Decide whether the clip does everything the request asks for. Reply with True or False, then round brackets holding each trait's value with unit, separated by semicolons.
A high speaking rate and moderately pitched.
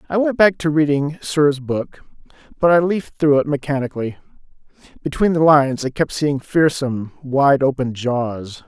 False (160 wpm; 145 Hz)